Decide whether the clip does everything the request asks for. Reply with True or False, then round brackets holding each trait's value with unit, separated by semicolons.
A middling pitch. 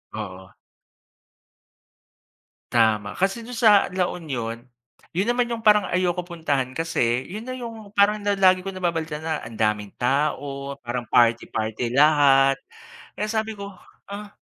True (160 Hz)